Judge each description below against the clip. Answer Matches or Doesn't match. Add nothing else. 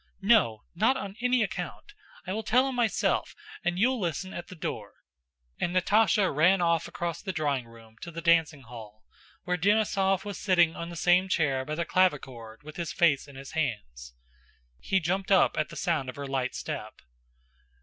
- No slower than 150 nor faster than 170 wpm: Doesn't match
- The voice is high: Doesn't match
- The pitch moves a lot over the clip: Matches